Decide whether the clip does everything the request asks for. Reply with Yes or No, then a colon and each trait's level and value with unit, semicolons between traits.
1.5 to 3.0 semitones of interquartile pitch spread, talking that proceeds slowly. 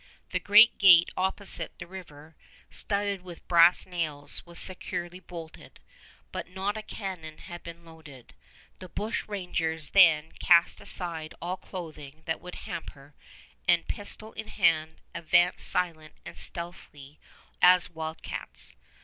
Yes: average, 2.7 semitones; slow, 130 wpm